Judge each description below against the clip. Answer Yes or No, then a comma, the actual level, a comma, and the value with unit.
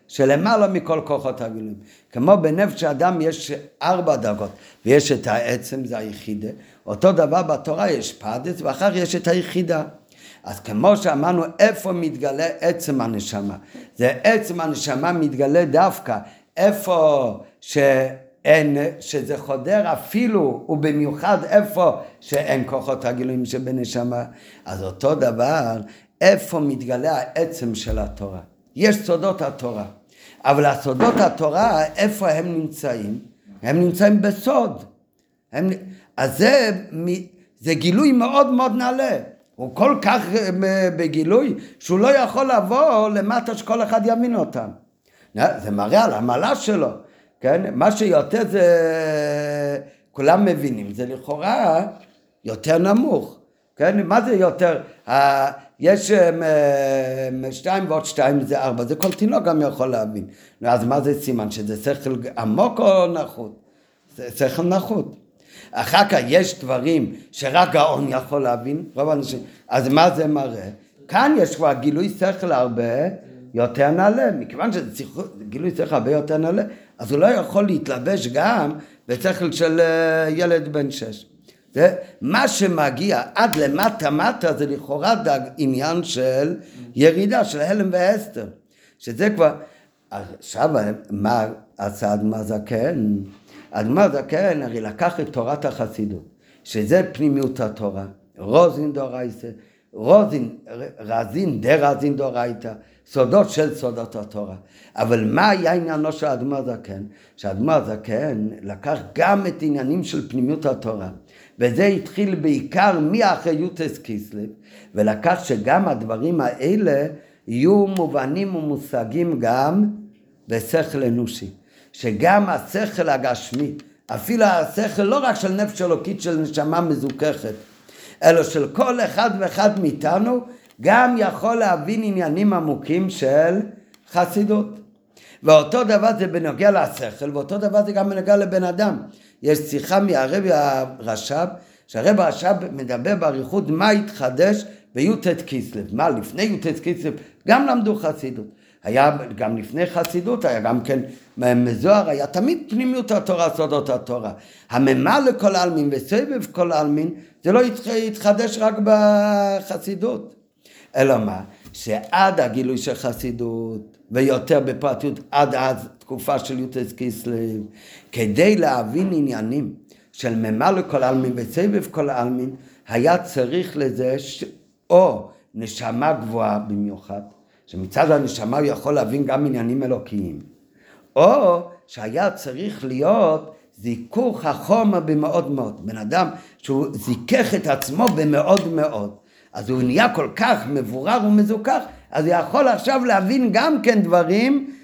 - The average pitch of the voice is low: No, medium, 150 Hz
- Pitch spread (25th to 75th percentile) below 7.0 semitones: No, wide, 7.4 semitones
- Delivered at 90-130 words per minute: Yes, average, 125 wpm